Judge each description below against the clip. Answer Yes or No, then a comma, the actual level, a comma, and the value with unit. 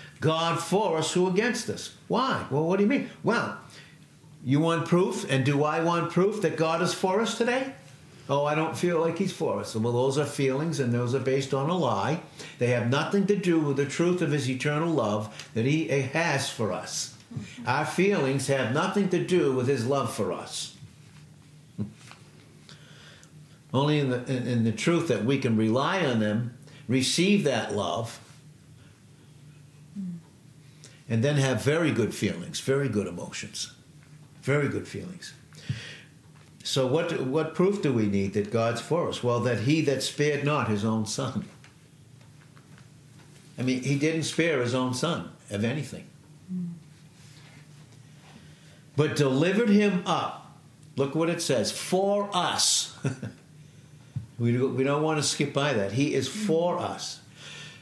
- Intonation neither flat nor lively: Yes, average, 3.3 semitones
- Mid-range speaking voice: Yes, medium, 145 Hz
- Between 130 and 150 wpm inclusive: No, average, 160 wpm